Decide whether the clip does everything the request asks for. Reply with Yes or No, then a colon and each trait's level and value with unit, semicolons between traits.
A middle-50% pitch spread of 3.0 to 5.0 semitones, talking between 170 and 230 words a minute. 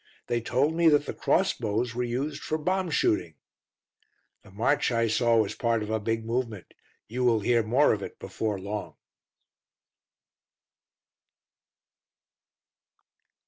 No: average, 3.6 semitones; slow, 135 wpm